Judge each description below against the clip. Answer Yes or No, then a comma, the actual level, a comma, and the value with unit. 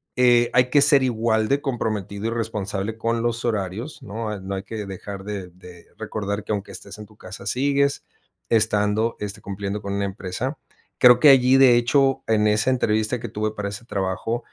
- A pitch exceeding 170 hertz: No, low, 110 Hz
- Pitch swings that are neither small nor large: Yes, average, 3.2 semitones